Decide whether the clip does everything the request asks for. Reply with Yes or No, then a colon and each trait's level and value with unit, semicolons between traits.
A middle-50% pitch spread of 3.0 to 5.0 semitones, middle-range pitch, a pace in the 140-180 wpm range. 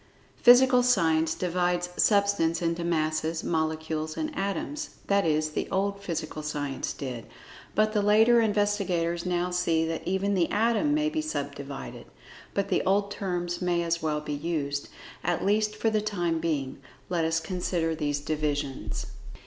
Yes: average, 4.2 semitones; medium, 175 Hz; average, 150 wpm